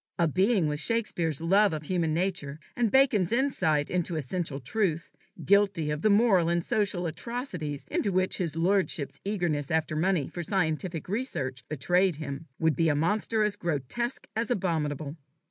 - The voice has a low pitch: No, medium, 175 Hz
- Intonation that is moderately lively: Yes, average, 4.7 semitones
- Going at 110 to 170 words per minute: Yes, average, 160 wpm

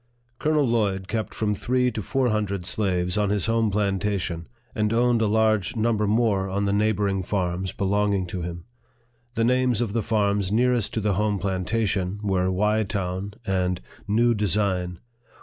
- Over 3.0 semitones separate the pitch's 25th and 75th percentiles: No, narrow, 2.6 semitones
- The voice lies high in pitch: No, low, 105 Hz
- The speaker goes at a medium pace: Yes, average, 165 wpm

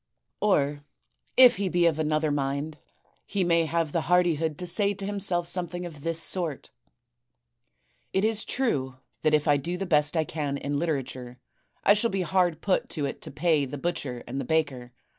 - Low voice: No, medium, 160 Hz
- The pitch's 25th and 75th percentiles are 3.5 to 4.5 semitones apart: Yes, average, 3.8 semitones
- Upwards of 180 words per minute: Yes, average, 190 wpm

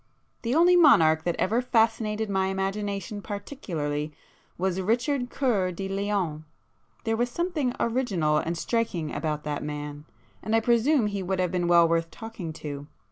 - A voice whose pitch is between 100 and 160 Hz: No, high, 195 Hz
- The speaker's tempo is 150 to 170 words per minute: Yes, average, 155 wpm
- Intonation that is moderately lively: No, wide, 5.7 semitones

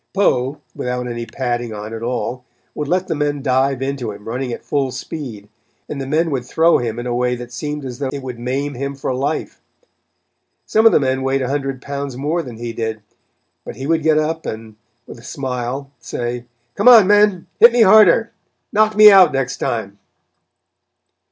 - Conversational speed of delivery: Yes, average, 195 wpm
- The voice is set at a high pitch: No, low, 135 Hz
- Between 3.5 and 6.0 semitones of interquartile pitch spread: Yes, average, 3.9 semitones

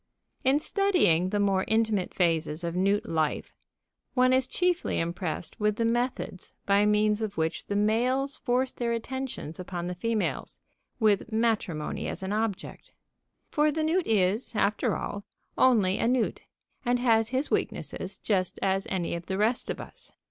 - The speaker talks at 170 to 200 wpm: No, average, 160 wpm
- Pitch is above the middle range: Yes, high, 215 Hz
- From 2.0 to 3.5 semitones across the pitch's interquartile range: No, average, 4.8 semitones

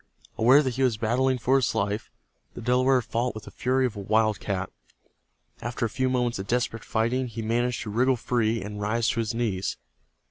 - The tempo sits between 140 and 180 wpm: No, average, 200 wpm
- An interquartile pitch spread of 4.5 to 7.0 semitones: No, narrow, 2.6 semitones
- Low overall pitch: Yes, low, 115 Hz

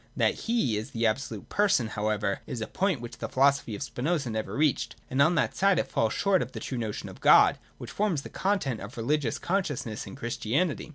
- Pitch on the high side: No, low, 130 Hz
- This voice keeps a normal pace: No, fast, 220 wpm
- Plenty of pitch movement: Yes, wide, 6.8 semitones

